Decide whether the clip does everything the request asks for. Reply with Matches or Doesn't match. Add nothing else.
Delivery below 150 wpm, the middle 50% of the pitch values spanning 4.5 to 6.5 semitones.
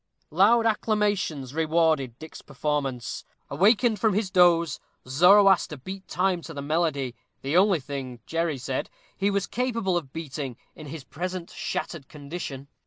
Matches